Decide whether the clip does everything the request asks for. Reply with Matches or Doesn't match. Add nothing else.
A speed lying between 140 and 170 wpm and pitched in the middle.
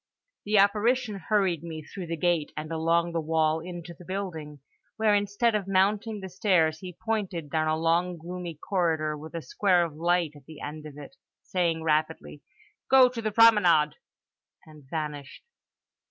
Matches